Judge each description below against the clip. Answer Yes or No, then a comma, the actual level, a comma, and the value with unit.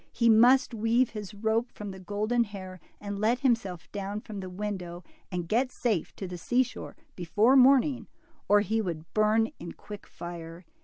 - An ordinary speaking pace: Yes, average, 175 wpm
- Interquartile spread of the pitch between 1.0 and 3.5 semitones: No, average, 3.9 semitones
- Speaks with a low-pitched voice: No, high, 210 Hz